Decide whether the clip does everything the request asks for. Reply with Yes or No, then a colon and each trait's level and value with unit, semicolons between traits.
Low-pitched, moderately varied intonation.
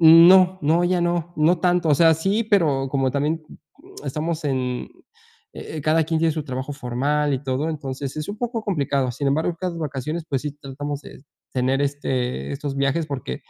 No: medium, 150 Hz; average, 3.5 semitones